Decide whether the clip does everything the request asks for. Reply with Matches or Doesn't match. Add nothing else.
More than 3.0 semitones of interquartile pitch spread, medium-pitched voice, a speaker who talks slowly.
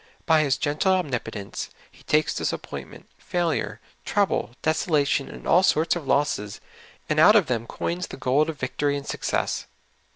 Doesn't match